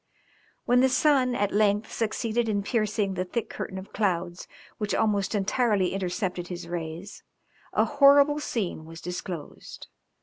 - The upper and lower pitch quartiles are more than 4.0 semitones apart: Yes, average, 4.6 semitones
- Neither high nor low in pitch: No, high, 205 Hz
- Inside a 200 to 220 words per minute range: No, average, 140 wpm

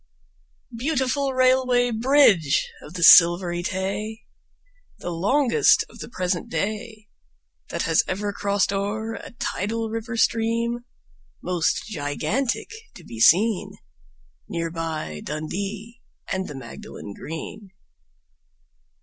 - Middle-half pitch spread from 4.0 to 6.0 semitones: Yes, average, 5.1 semitones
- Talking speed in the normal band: No, slow, 105 wpm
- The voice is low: No, high, 205 Hz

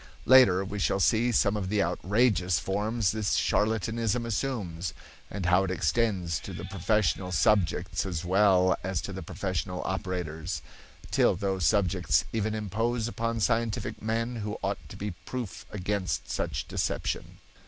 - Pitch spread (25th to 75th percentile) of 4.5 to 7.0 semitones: No, average, 3.4 semitones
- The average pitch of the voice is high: No, low, 100 Hz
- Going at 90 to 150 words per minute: Yes, average, 145 wpm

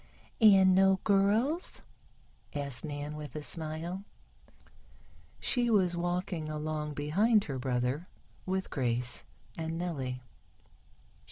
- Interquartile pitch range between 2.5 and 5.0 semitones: Yes, average, 4.7 semitones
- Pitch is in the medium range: Yes, medium, 160 Hz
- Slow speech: Yes, slow, 100 wpm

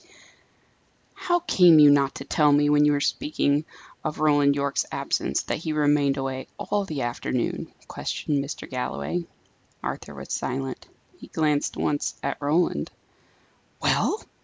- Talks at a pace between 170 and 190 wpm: No, average, 140 wpm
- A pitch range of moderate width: No, narrow, 2.0 semitones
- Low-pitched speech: No, medium, 145 Hz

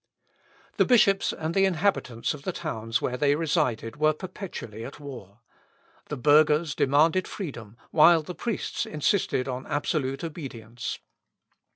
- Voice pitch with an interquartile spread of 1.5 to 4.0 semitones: No, average, 5.1 semitones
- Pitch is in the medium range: Yes, medium, 150 Hz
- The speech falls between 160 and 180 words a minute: No, slow, 135 wpm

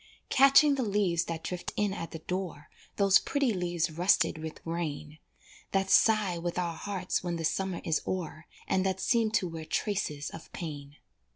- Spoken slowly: No, average, 175 wpm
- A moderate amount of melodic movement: Yes, average, 3.3 semitones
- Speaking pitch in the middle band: Yes, medium, 180 Hz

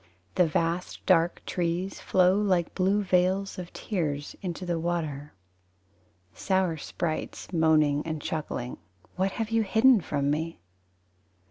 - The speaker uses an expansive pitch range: No, average, 3.1 semitones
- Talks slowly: Yes, slow, 125 wpm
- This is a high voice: No, medium, 175 Hz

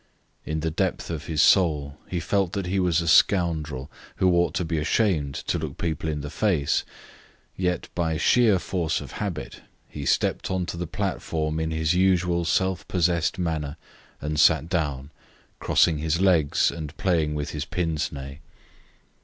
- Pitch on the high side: No, very low, 80 Hz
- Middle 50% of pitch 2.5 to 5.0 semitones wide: Yes, average, 2.9 semitones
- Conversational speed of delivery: Yes, average, 170 wpm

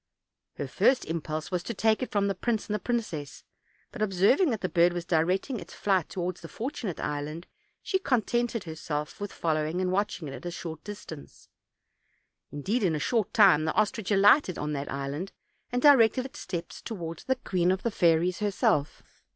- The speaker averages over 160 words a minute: Yes, average, 185 wpm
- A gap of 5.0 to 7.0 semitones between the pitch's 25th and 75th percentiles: Yes, wide, 5.4 semitones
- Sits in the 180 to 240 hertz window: Yes, medium, 185 Hz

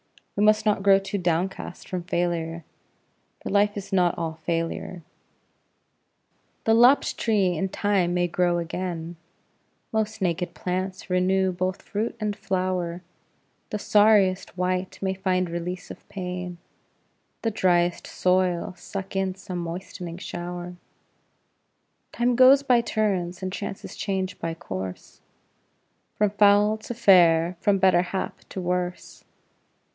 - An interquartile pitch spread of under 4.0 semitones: Yes, narrow, 2.4 semitones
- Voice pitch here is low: No, medium, 185 Hz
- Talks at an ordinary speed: No, slow, 130 wpm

